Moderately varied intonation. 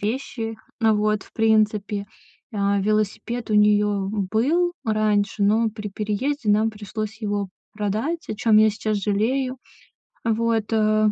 No: narrow, 1.4 semitones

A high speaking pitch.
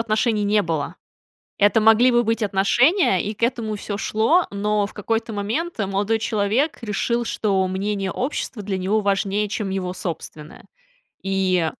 Yes: high, 210 Hz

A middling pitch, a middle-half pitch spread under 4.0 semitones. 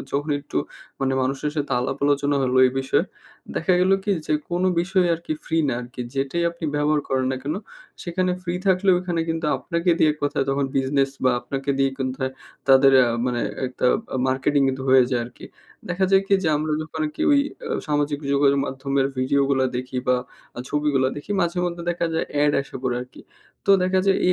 No: medium, 145 Hz; average, 4.3 semitones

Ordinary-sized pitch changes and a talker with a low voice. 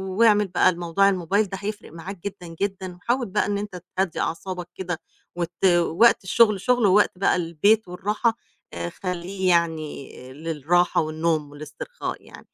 No: average, 3.3 semitones; medium, 180 Hz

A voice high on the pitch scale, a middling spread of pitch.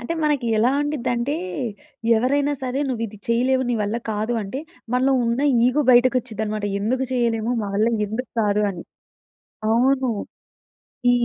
Yes: high, 240 Hz; average, 3.0 semitones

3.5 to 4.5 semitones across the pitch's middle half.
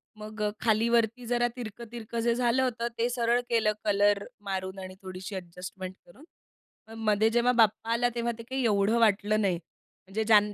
No: average, 2.7 semitones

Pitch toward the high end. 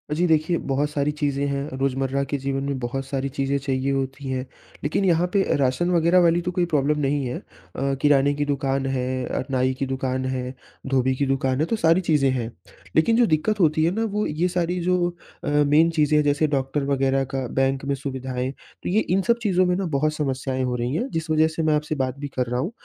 No: medium, 140 Hz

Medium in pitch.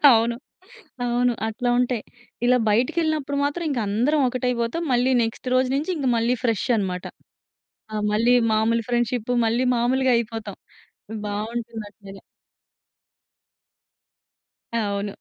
No: high, 235 Hz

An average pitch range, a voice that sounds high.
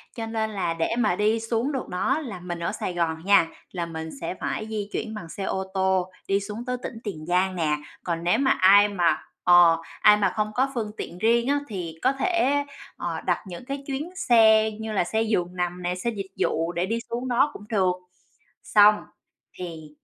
Yes: average, 4.3 semitones; high, 200 Hz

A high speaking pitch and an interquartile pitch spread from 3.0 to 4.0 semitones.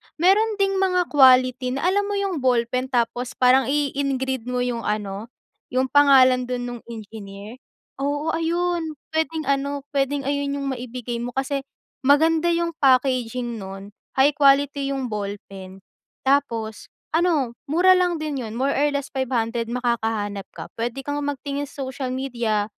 Yes: very high, 265 Hz; average, 3.4 semitones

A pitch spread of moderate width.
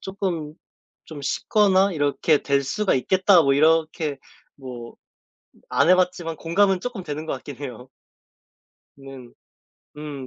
Yes: average, 4.9 semitones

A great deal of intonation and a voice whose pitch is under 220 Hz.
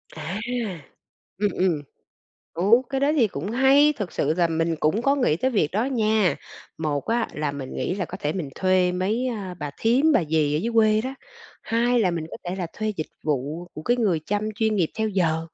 Yes: wide, 6.1 semitones; high, 190 Hz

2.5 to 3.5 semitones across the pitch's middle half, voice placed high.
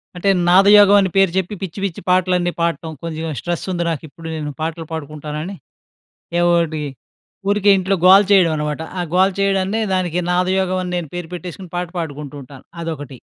No: average, 2.8 semitones; medium, 175 Hz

